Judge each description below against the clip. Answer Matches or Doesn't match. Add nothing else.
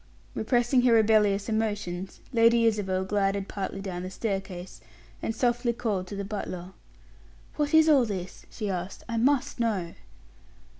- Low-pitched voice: Doesn't match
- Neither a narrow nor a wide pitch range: Matches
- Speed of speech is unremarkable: Matches